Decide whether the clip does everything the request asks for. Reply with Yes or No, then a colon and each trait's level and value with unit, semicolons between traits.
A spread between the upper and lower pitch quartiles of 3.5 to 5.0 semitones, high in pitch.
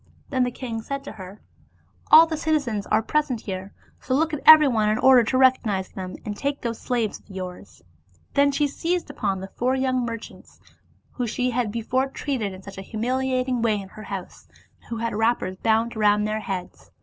Yes: average, 4.0 semitones; high, 235 Hz